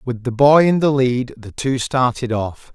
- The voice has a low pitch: Yes, low, 125 Hz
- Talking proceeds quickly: Yes, fast, 220 wpm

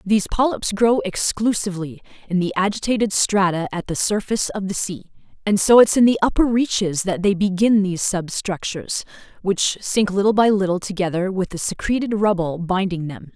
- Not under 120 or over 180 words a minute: Yes, average, 170 wpm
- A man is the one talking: No, female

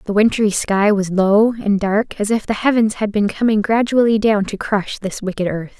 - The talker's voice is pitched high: Yes, high, 210 Hz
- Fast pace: Yes, fast, 215 wpm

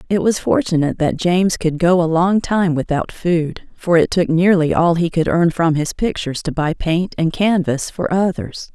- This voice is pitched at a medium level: Yes, medium, 170 Hz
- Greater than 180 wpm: Yes, fast, 205 wpm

